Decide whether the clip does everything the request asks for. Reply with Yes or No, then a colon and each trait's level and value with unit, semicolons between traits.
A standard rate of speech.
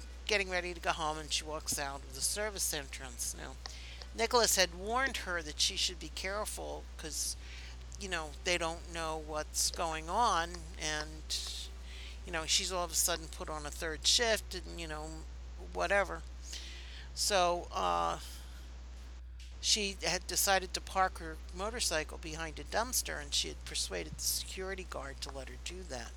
Yes: average, 165 wpm